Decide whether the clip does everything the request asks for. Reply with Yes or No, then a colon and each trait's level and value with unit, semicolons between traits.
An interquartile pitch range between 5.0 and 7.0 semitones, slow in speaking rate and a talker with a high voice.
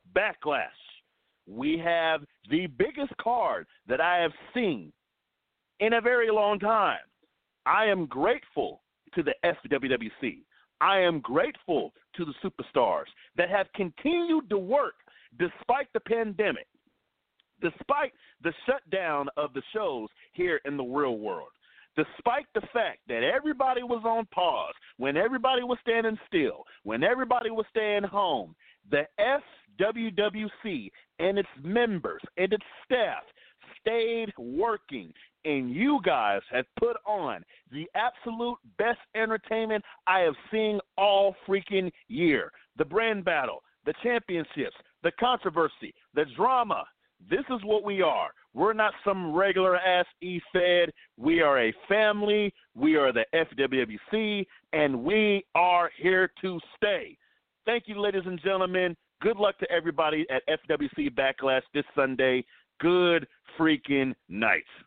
Yes: wide, 5.5 semitones; slow, 130 wpm; high, 205 Hz